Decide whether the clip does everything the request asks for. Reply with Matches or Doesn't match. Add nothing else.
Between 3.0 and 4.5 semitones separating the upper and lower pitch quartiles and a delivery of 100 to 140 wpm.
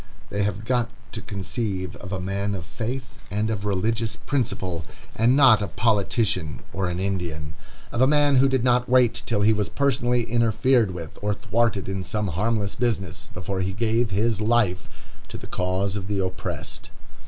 Doesn't match